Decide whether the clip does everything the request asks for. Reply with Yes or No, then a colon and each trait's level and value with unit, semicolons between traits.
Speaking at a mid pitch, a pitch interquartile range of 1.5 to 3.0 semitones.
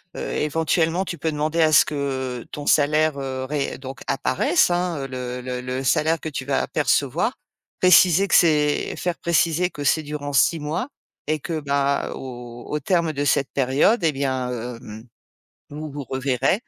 No: medium, 145 Hz; average, 3.4 semitones